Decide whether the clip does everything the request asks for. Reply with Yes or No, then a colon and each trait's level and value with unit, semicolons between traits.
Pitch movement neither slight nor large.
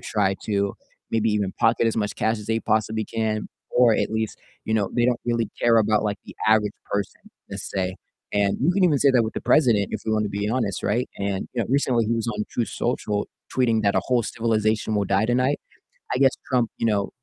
No: narrow, 2.3 semitones